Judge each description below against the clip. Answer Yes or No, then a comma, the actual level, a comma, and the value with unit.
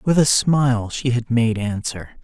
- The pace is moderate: Yes, average, 190 wpm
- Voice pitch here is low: Yes, low, 120 Hz